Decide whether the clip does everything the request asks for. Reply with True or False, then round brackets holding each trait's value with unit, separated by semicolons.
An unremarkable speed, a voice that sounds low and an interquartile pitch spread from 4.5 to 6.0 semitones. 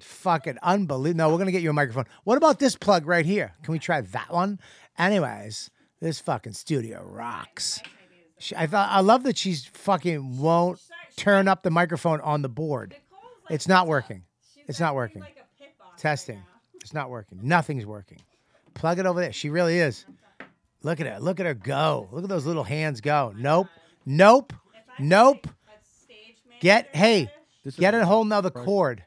False (170 wpm; 170 Hz; 5.1 semitones)